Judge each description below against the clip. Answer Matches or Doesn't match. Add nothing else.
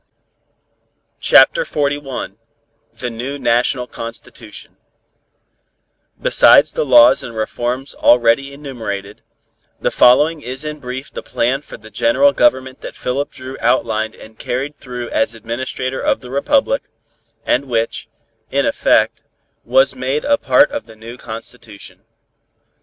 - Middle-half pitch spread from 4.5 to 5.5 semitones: Doesn't match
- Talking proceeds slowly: Matches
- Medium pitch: Doesn't match